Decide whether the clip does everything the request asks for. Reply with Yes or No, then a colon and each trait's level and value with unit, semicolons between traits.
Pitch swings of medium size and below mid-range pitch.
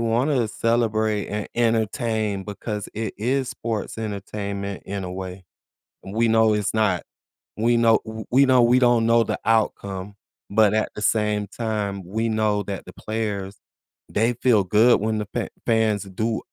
No: narrow, 2.1 semitones; low, 110 Hz